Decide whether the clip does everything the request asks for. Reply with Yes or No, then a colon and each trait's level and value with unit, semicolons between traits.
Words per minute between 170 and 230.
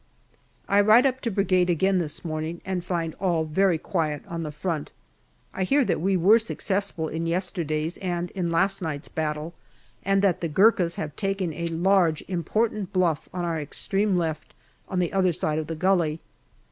Yes: average, 180 wpm